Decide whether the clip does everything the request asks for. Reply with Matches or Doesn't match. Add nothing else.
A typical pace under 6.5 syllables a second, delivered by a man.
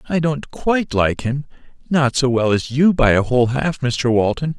Matches